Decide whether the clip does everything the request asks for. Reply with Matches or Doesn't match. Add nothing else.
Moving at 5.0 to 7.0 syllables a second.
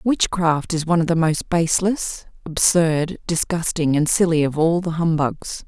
Doesn't match